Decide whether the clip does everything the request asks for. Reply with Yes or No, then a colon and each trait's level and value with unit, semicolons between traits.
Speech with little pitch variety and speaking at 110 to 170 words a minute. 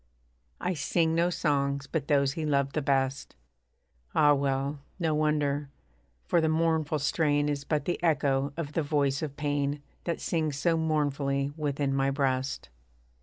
Yes: narrow, 2.2 semitones; average, 155 wpm